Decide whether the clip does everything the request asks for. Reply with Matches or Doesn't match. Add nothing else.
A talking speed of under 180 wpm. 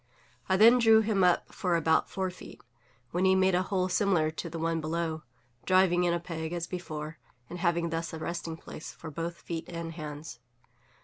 Doesn't match